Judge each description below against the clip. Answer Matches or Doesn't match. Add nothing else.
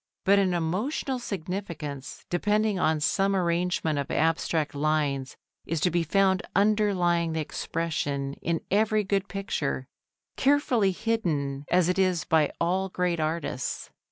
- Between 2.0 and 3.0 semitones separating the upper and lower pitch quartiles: Doesn't match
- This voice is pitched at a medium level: Matches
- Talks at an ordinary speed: Doesn't match